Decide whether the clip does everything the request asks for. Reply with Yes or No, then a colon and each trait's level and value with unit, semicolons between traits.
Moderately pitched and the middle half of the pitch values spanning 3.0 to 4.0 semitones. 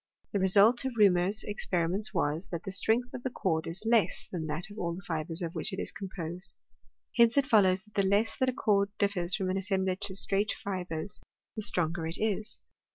No: high, 195 Hz; average, 3.3 semitones